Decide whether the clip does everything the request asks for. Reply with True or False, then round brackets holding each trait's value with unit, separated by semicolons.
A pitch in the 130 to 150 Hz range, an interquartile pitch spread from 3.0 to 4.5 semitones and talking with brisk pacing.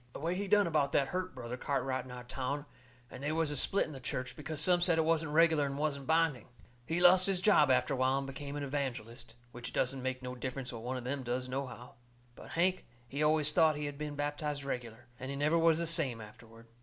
True (140 Hz; 3.9 semitones; 245 wpm)